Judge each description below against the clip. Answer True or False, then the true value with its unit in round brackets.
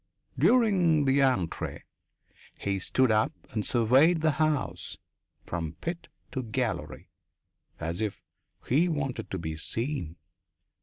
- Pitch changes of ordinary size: False (7.5 semitones)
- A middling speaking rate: False (115 wpm)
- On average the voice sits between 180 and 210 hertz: False (130 Hz)